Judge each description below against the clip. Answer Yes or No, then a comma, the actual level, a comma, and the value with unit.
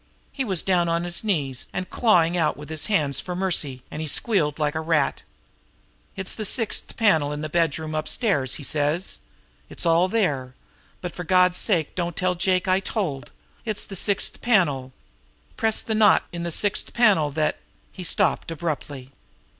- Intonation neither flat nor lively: Yes, average, 4.2 semitones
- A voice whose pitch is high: No, medium, 170 Hz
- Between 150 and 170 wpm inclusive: No, average, 180 wpm